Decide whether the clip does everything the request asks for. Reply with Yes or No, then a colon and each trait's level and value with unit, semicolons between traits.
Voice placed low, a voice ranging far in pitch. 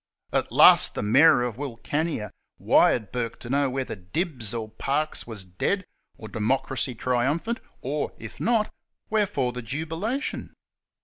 Yes: low, 130 Hz; wide, 6.0 semitones